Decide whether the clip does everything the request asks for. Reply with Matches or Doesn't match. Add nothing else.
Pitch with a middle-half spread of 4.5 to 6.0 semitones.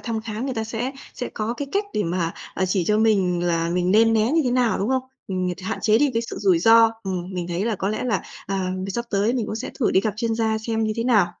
Doesn't match